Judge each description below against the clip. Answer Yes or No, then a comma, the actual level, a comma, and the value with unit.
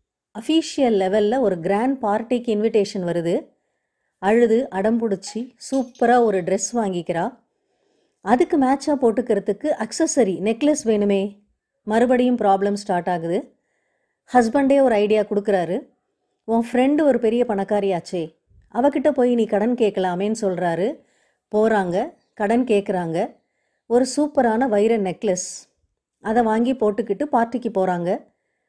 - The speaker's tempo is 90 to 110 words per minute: Yes, average, 105 wpm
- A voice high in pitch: Yes, high, 220 Hz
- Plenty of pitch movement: No, average, 4.0 semitones